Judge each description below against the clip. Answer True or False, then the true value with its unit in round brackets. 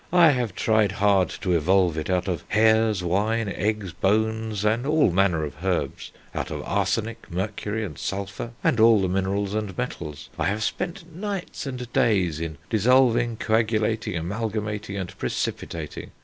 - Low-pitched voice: True (105 Hz)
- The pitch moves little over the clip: False (3.4 semitones)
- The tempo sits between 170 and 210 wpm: False (155 wpm)